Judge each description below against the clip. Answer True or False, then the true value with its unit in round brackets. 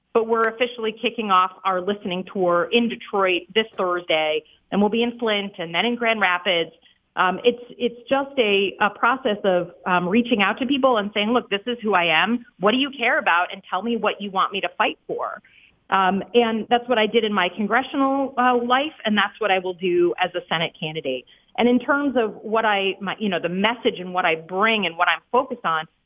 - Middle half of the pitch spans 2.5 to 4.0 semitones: False (4.6 semitones)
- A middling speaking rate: False (230 wpm)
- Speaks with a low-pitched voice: False (210 Hz)